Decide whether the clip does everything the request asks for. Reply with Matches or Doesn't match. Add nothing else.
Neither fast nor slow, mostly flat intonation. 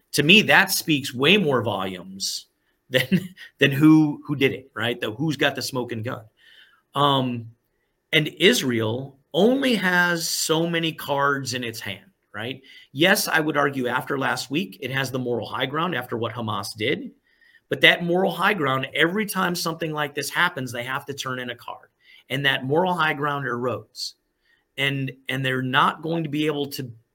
Doesn't match